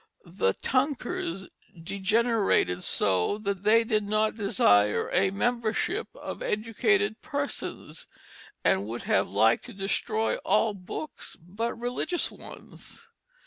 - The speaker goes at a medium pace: No, slow, 110 wpm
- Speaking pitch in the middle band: No, high, 210 Hz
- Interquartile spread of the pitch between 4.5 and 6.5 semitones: Yes, average, 4.9 semitones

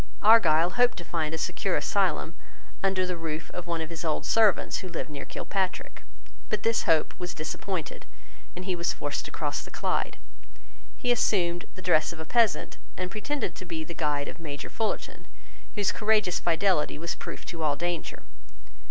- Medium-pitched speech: Yes, medium, 175 Hz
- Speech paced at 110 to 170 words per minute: No, average, 180 wpm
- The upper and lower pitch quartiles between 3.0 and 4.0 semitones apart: Yes, average, 3.3 semitones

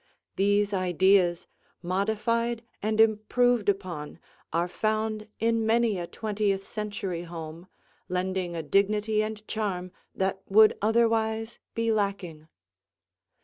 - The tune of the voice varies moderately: Yes, average, 3.1 semitones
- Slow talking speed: Yes, slow, 105 wpm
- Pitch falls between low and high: No, high, 205 Hz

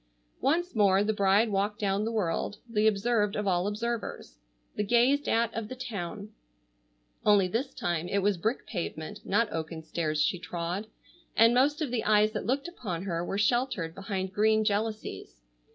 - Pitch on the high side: Yes, high, 210 Hz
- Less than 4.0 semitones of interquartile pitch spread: Yes, average, 3.6 semitones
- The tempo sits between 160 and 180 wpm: Yes, average, 170 wpm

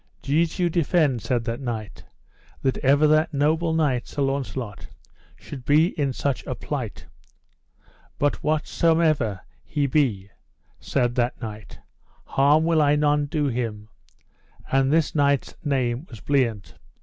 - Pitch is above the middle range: No, medium, 140 Hz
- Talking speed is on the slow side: Yes, slow, 130 wpm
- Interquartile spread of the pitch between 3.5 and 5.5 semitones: Yes, average, 4.0 semitones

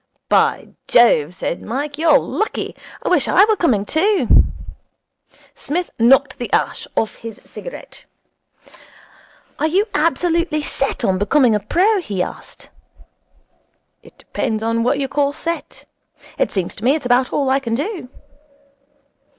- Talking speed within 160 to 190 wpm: No, average, 140 wpm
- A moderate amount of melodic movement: No, wide, 6.4 semitones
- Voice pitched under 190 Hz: No, very high, 275 Hz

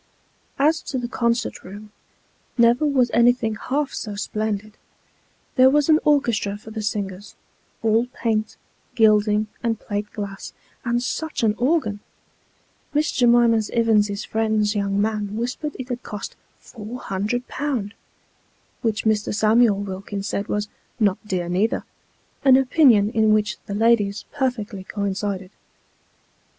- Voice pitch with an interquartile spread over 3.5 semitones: No, average, 3.0 semitones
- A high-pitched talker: Yes, high, 220 Hz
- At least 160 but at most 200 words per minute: No, slow, 135 wpm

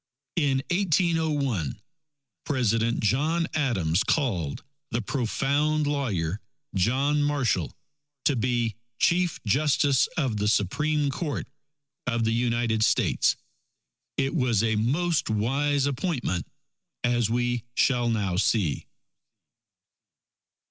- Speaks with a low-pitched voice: Yes, low, 125 Hz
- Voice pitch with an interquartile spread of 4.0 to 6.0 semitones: Yes, average, 4.9 semitones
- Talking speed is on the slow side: Yes, slow, 100 wpm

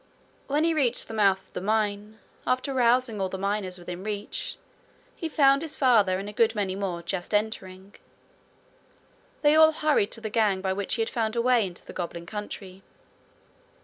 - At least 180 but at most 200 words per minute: Yes, average, 185 wpm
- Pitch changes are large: No, average, 4.5 semitones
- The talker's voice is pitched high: Yes, high, 210 Hz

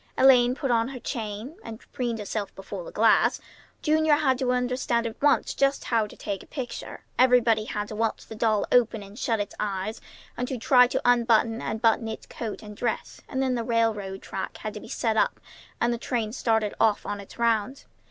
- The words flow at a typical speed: No, fast, 210 wpm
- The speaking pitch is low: No, high, 230 Hz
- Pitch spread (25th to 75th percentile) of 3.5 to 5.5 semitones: No, narrow, 2.6 semitones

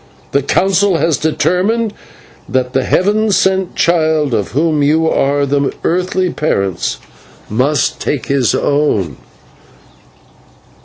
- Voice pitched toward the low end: No, medium, 155 Hz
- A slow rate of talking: Yes, slow, 110 wpm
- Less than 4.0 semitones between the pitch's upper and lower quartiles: No, average, 4.8 semitones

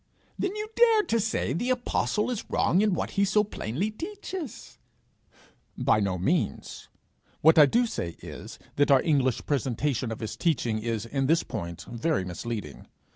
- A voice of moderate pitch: Yes, medium, 150 Hz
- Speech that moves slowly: No, average, 165 wpm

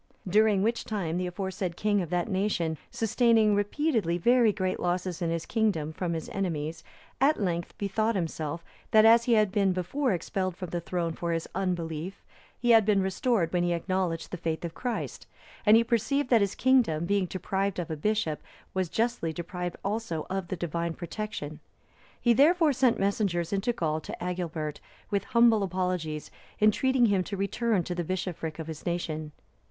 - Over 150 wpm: Yes, average, 180 wpm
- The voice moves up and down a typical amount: Yes, average, 4.3 semitones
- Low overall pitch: No, medium, 185 Hz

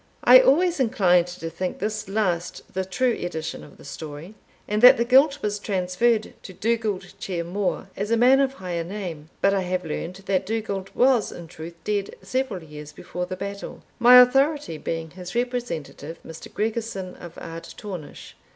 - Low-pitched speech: No, high, 195 Hz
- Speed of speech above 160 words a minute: Yes, average, 170 wpm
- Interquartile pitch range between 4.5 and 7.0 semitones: Yes, average, 5.0 semitones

